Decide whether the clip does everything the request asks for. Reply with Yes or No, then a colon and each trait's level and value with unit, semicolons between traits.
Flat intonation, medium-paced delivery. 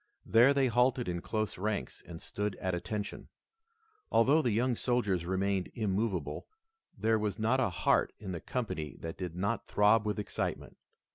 No: average, 3.8 semitones; average, 160 wpm